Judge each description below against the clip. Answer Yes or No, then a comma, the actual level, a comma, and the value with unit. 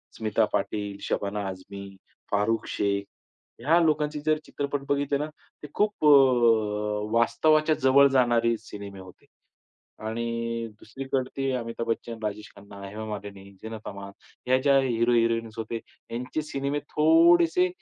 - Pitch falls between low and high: No, low, 115 Hz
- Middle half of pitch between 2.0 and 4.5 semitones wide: No, average, 5.0 semitones